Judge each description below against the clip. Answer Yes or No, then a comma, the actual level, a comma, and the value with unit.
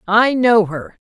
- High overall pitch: Yes, high, 215 Hz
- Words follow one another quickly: No, average, 170 wpm